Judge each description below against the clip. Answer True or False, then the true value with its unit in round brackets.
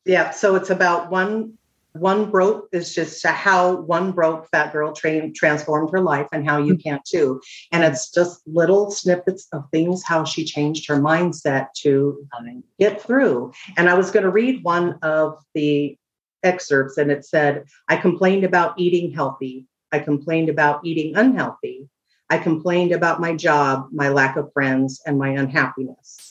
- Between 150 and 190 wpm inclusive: True (165 wpm)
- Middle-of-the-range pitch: True (160 Hz)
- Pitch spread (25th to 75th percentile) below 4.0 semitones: True (3.5 semitones)